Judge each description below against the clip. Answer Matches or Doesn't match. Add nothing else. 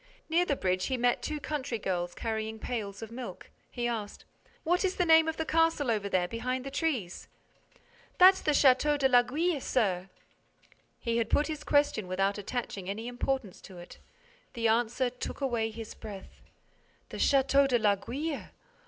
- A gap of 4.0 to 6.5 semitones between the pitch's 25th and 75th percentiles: Matches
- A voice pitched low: Doesn't match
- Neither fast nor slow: Matches